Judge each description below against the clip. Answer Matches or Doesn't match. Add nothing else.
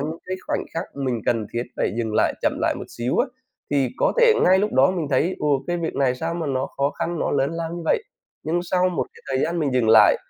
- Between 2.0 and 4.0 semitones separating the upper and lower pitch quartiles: Doesn't match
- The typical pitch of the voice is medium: Matches